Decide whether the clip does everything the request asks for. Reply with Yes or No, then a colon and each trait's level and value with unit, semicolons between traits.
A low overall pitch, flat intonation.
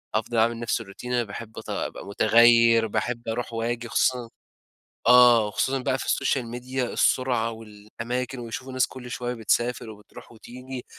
Yes: low, 120 Hz; narrow, 1.6 semitones